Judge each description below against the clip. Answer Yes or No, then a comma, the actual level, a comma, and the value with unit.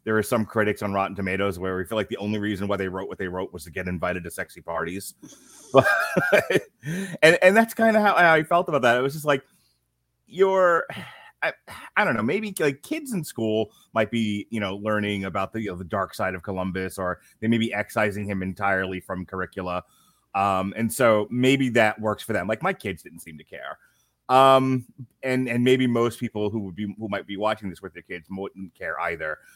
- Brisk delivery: Yes, fast, 225 wpm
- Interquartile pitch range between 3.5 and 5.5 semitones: Yes, average, 5.1 semitones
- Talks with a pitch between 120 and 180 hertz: No, low, 105 Hz